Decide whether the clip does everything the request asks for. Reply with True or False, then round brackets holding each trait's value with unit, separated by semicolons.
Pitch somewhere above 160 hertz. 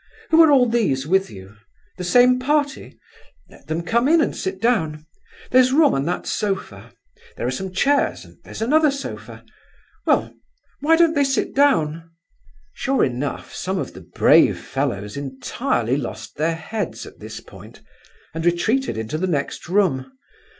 True (190 Hz)